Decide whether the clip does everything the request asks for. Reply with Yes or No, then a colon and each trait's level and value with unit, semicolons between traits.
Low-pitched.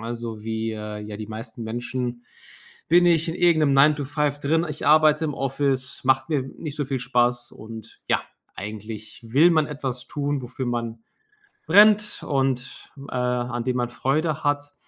Yes: low, 130 Hz